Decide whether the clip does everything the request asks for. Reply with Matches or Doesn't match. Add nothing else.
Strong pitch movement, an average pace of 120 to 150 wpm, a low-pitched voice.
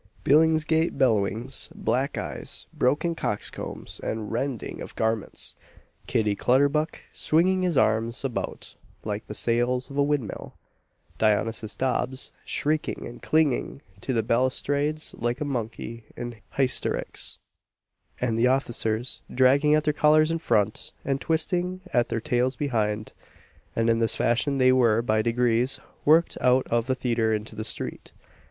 Doesn't match